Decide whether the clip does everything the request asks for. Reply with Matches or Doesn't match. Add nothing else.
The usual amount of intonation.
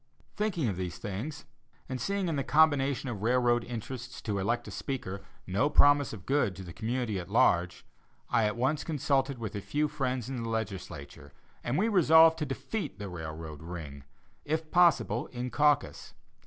Doesn't match